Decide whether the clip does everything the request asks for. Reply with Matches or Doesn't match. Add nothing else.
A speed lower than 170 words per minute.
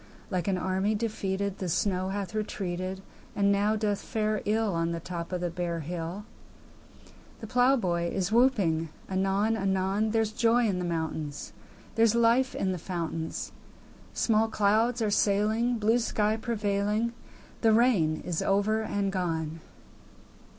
Matches